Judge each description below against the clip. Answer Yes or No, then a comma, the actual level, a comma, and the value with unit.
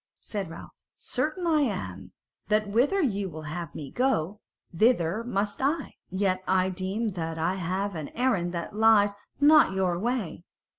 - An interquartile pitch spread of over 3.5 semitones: Yes, average, 4.9 semitones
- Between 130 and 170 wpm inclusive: Yes, average, 155 wpm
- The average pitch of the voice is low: No, high, 195 Hz